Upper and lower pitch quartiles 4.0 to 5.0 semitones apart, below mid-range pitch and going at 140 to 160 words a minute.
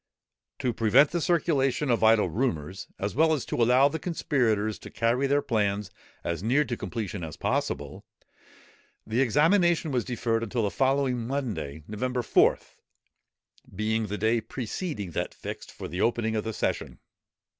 Yes: average, 4.3 semitones; low, 115 Hz; average, 155 wpm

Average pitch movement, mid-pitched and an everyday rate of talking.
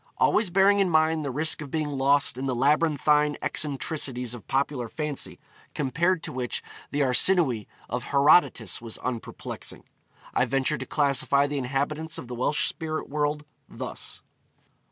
Yes: average, 3.2 semitones; medium, 145 Hz; average, 155 wpm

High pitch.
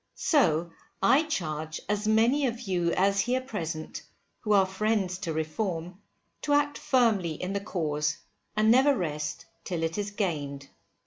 Yes: high, 195 Hz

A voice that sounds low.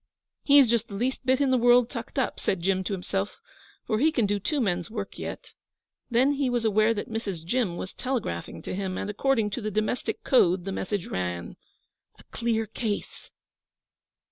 No: high, 215 Hz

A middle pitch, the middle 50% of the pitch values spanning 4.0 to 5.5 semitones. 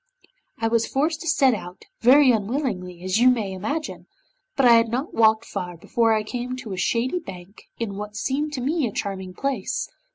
No: high, 230 Hz; average, 4.9 semitones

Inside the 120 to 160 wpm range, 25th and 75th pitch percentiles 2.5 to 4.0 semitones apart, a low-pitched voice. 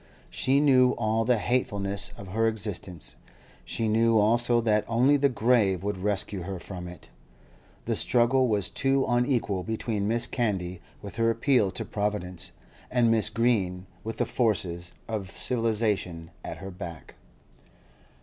Yes: average, 145 wpm; average, 3.6 semitones; low, 110 Hz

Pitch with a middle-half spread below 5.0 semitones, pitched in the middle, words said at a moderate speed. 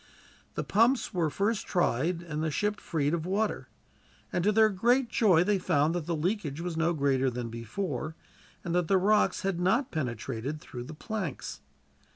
No: wide, 5.4 semitones; medium, 170 Hz; average, 180 wpm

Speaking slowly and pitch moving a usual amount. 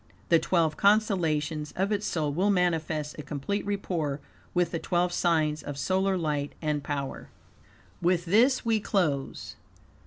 No: average, 145 wpm; average, 4.2 semitones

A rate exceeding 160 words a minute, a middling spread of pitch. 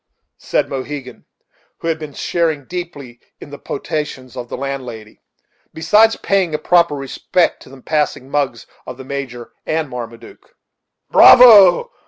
No: average, 140 wpm; average, 4.5 semitones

